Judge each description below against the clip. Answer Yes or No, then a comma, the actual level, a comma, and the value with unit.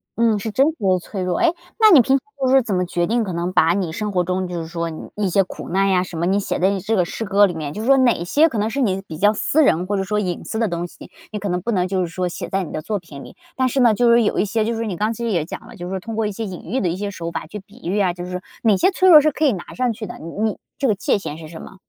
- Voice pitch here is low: No, high, 200 Hz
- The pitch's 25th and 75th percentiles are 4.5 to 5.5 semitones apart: No, average, 4.1 semitones